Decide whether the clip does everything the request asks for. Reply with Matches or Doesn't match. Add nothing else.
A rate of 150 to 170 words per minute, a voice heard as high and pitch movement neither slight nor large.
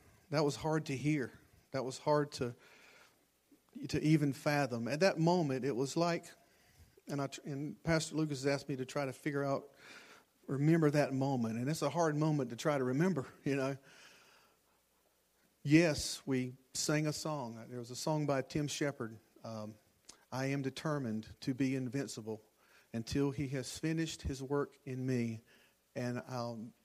Doesn't match